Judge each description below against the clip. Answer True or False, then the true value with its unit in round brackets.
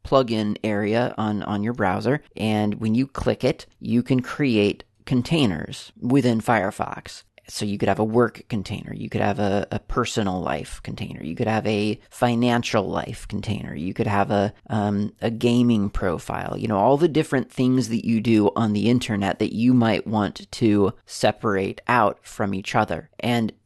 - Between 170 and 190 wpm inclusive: True (180 wpm)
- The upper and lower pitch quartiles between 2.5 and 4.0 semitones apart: True (2.9 semitones)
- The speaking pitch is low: True (110 Hz)